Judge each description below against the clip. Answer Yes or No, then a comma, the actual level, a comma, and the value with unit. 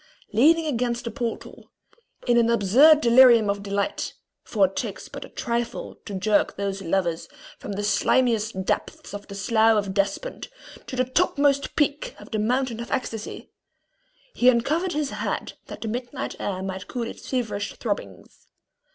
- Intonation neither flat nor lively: Yes, average, 4.2 semitones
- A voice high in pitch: Yes, high, 230 Hz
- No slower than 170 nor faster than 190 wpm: No, average, 160 wpm